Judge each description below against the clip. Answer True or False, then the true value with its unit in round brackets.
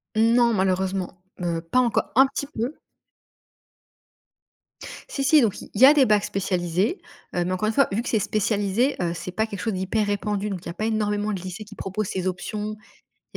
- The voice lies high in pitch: True (205 Hz)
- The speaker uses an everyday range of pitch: True (3.1 semitones)